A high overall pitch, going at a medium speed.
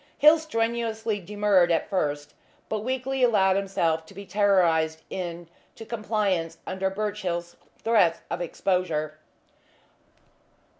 No: high, 195 Hz; slow, 105 wpm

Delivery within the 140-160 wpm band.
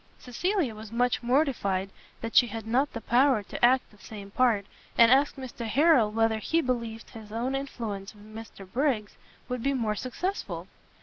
No: average, 175 wpm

